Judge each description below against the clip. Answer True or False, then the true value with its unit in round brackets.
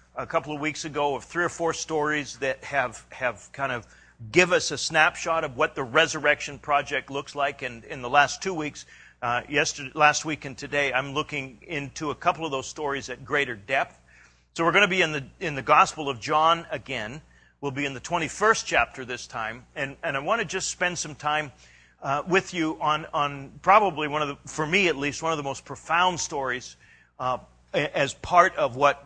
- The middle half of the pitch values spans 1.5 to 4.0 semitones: True (2.8 semitones)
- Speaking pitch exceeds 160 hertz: False (150 Hz)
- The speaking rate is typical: False (220 wpm)